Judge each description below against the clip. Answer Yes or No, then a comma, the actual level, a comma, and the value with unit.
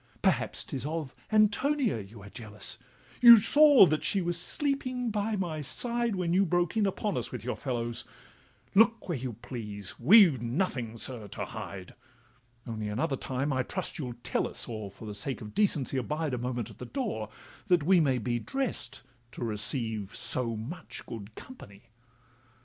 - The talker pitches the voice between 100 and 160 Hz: Yes, low, 135 Hz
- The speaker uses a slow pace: No, average, 170 wpm